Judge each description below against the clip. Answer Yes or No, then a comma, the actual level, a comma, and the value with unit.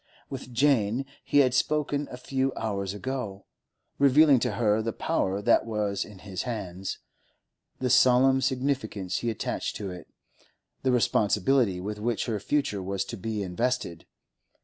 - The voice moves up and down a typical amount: Yes, average, 4.6 semitones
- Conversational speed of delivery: Yes, average, 150 wpm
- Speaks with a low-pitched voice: Yes, low, 115 Hz